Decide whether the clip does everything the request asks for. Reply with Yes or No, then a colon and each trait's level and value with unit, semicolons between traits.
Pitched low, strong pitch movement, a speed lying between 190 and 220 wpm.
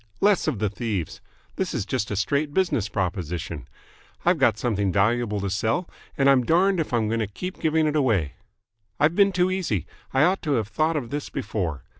Yes: low, 120 Hz; wide, 7.7 semitones; average, 200 wpm